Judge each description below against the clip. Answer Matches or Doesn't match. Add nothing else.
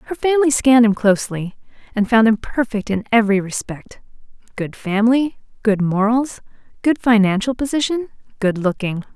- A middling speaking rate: Doesn't match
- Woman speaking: Matches